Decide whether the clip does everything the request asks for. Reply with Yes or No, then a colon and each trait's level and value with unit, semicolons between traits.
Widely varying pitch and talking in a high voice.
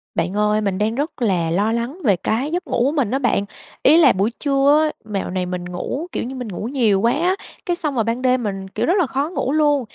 Yes: wide, 6.0 semitones; high, 240 Hz